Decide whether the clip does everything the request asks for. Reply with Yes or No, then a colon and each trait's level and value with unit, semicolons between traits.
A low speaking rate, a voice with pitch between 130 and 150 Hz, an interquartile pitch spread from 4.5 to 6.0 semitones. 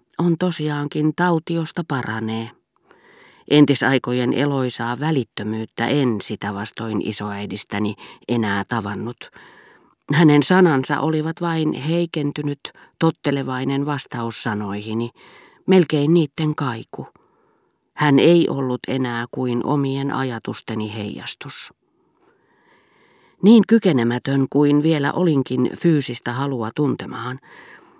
Yes: slow, 85 wpm; low, 135 Hz; average, 4.8 semitones